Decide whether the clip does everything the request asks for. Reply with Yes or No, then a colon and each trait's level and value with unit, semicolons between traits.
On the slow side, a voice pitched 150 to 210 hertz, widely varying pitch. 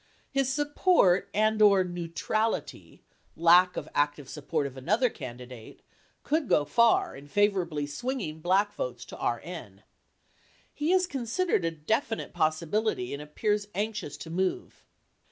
Yes: slow, 125 wpm; high, 190 Hz; wide, 6.8 semitones